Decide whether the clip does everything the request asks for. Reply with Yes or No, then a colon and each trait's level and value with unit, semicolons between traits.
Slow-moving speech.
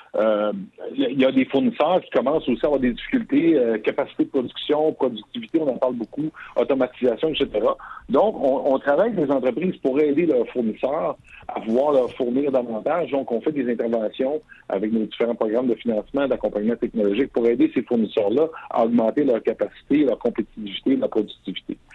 No: average, 180 wpm